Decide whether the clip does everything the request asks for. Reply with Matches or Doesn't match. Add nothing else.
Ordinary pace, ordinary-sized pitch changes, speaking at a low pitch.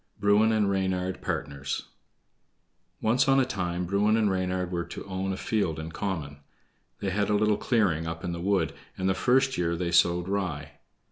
Matches